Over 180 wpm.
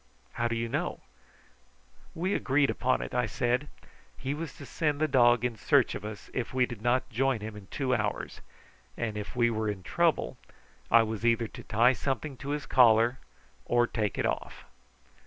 Yes: average, 190 wpm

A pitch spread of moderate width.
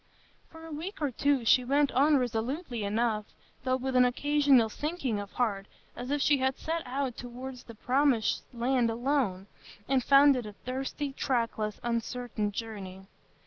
Yes: average, 3.5 semitones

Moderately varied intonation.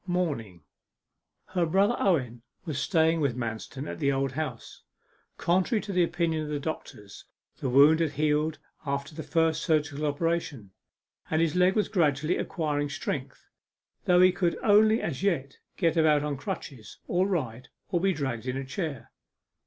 Yes: average, 4.1 semitones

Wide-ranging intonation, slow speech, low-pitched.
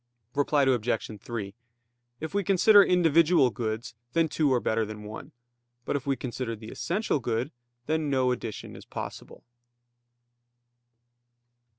Yes: wide, 5.9 semitones; slow, 130 wpm; low, 130 Hz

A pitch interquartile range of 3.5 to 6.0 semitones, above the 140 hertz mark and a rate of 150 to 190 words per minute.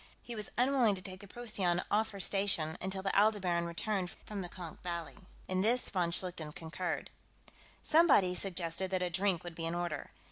No: average, 2.9 semitones; medium, 185 Hz; average, 185 wpm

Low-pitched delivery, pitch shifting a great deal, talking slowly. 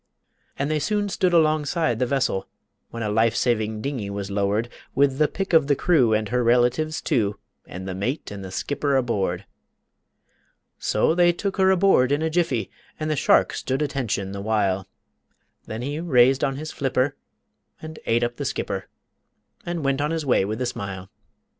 No: low, 130 Hz; wide, 6.2 semitones; average, 180 wpm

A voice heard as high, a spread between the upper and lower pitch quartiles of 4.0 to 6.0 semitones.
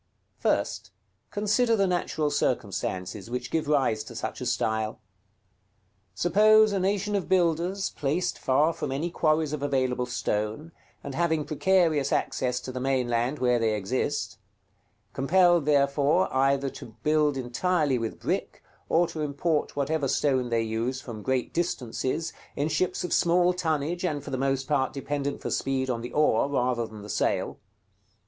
No: medium, 140 Hz; average, 4.9 semitones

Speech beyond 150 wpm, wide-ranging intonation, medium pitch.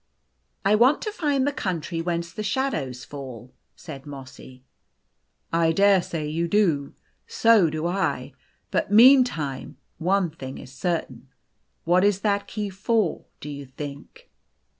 No: average, 140 wpm; wide, 6.3 semitones; medium, 170 Hz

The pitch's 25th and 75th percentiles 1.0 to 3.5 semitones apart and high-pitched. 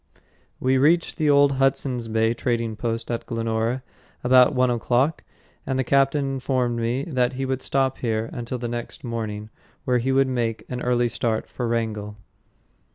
No: narrow, 2.5 semitones; low, 125 Hz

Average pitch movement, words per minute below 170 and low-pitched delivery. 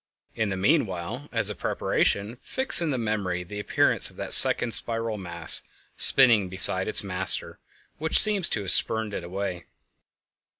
Yes: average, 4.2 semitones; average, 160 wpm; low, 105 Hz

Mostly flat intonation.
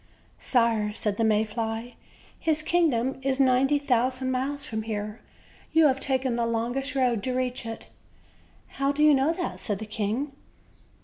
No: average, 3.3 semitones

